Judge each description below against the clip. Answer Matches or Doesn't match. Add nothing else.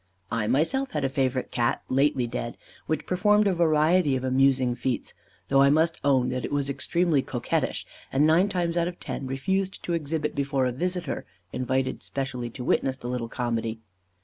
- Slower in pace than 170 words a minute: Doesn't match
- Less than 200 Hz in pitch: Matches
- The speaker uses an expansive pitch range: Doesn't match